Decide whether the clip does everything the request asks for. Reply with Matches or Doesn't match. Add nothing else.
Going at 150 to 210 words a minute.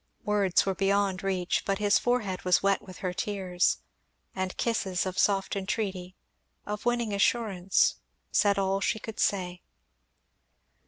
Doesn't match